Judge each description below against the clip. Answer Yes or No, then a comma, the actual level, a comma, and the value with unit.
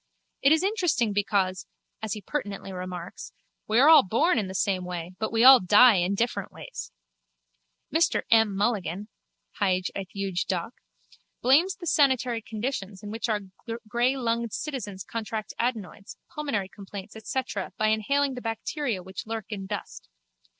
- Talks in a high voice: Yes, high, 215 Hz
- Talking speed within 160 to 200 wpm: No, average, 150 wpm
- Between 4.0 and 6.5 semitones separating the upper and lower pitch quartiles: Yes, average, 4.4 semitones